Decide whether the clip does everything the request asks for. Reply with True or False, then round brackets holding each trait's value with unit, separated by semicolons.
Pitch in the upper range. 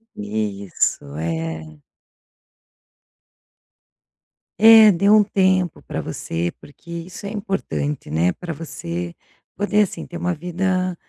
False (170 Hz)